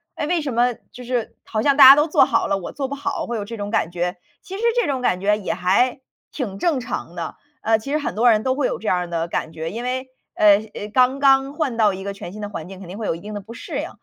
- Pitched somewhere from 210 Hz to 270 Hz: Yes, high, 230 Hz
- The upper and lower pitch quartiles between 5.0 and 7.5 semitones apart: Yes, wide, 5.5 semitones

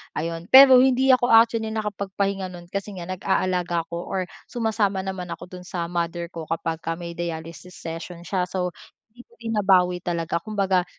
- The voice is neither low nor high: Yes, medium, 180 Hz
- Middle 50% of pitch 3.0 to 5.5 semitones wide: Yes, average, 3.3 semitones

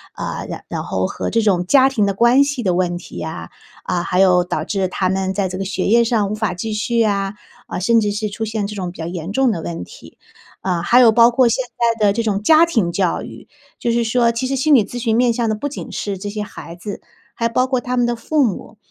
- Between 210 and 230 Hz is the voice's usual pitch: Yes, high, 215 Hz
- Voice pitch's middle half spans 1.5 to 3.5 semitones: No, average, 4.0 semitones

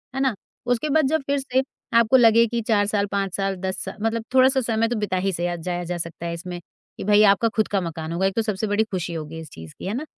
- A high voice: Yes, high, 200 Hz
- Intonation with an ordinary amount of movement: Yes, average, 4.5 semitones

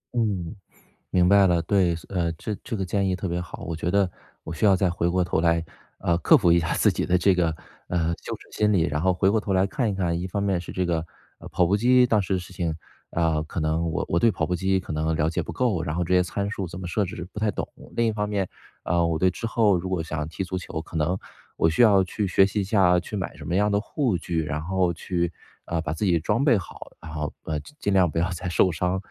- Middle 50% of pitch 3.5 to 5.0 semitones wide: No, average, 2.9 semitones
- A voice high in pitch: No, very low, 90 Hz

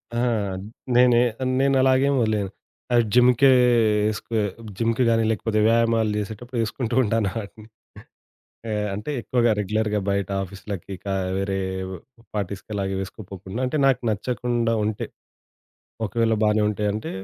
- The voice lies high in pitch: No, low, 110 Hz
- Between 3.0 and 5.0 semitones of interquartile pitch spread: No, narrow, 2.6 semitones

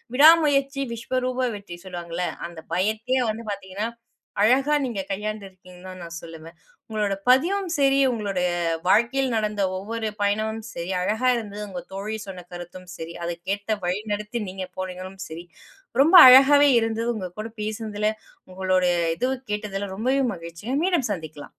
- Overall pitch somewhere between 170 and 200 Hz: No, high, 210 Hz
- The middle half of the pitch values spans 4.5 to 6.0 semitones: Yes, average, 4.9 semitones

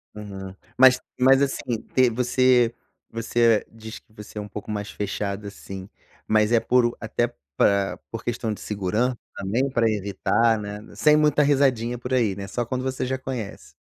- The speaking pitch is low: Yes, low, 115 Hz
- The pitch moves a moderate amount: Yes, average, 3.4 semitones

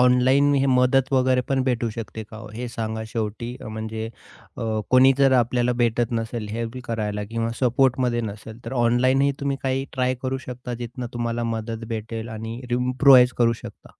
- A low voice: Yes, low, 120 Hz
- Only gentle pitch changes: Yes, narrow, 2.2 semitones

